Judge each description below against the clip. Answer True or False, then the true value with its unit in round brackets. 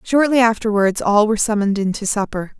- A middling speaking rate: True (185 wpm)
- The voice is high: True (215 Hz)